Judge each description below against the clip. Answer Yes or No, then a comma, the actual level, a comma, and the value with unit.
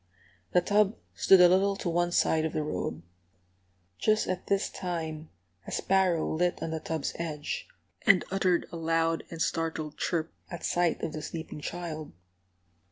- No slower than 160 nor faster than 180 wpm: Yes, average, 165 wpm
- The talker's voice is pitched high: No, medium, 170 Hz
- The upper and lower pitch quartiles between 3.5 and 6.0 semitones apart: No, narrow, 2.4 semitones